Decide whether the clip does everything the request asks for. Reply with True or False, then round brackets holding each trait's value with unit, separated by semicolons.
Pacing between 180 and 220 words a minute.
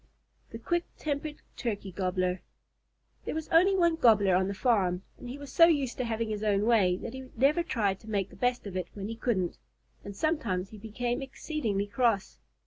True (200 wpm)